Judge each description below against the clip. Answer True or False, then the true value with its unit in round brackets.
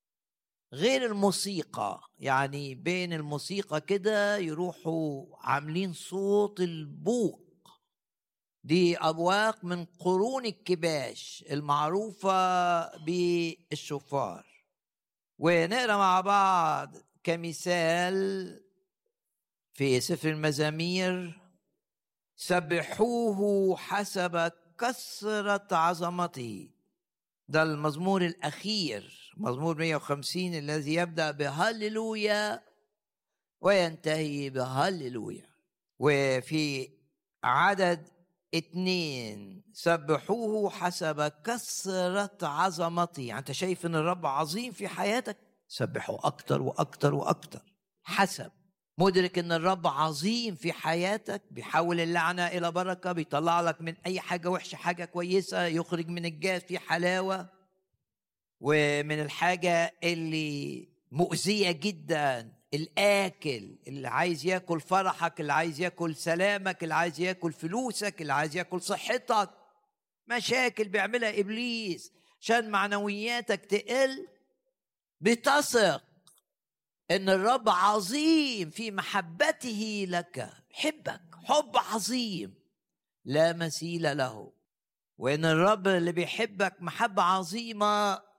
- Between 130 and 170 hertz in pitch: False (180 Hz)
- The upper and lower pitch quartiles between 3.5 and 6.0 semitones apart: True (3.8 semitones)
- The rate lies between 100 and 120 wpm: False (85 wpm)